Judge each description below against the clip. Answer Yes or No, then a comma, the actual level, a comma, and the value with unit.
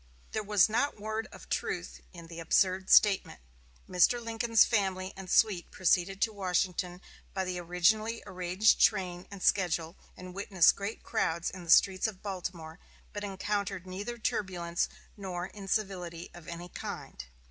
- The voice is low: No, medium, 185 Hz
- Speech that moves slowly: No, average, 150 wpm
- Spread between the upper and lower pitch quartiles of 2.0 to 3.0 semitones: Yes, average, 2.7 semitones